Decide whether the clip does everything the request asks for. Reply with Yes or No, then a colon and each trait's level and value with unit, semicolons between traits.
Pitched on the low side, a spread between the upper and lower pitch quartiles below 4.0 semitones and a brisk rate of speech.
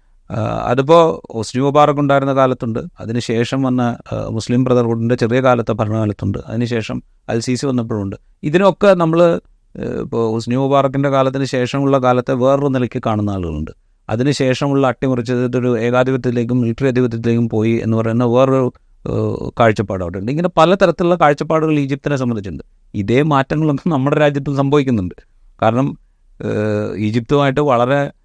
No: low, 125 Hz; average, 3.4 semitones; average, 110 wpm